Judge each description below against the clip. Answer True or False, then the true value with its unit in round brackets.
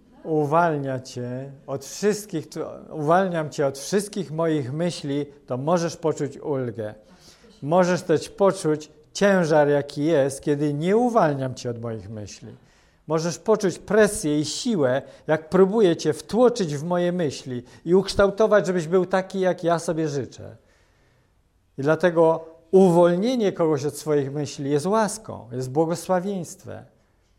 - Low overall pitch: False (155 Hz)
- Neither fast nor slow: False (130 wpm)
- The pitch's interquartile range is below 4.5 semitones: False (5.1 semitones)